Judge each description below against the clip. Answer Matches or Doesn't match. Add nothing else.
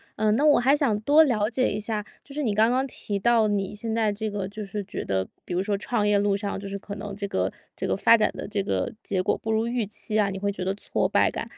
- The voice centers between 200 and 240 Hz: Matches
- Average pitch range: Doesn't match